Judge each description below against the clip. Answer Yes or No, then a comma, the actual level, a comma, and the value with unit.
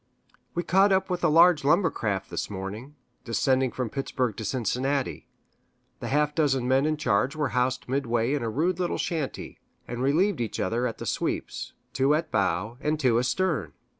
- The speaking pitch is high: No, low, 135 Hz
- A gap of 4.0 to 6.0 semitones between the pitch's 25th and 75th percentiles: Yes, average, 4.5 semitones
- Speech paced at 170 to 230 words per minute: Yes, average, 180 wpm